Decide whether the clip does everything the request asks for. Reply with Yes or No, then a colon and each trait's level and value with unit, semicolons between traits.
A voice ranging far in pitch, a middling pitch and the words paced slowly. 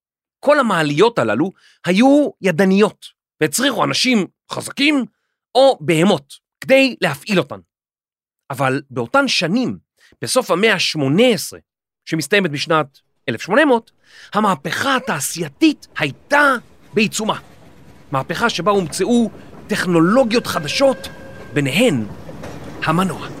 No: wide, 8.1 semitones; high, 200 Hz; slow, 85 wpm